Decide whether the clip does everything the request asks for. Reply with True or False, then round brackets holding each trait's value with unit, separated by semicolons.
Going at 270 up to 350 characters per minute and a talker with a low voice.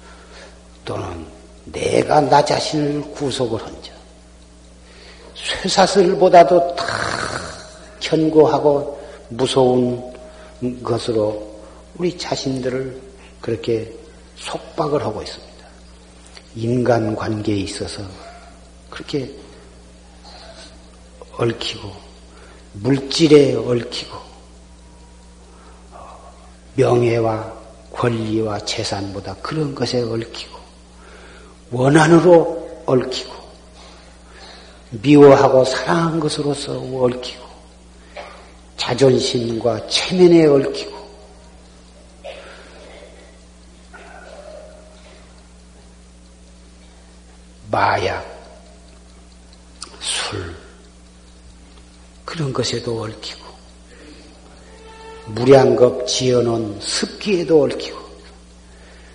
False (140 characters per minute; 100 Hz)